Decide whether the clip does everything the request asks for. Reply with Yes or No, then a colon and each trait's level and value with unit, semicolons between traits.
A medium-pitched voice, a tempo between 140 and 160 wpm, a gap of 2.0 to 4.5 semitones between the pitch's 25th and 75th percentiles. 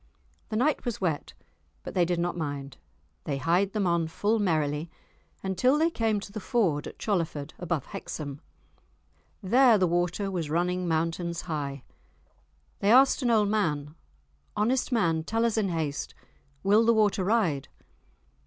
No: medium, 180 Hz; average, 155 wpm; average, 5.2 semitones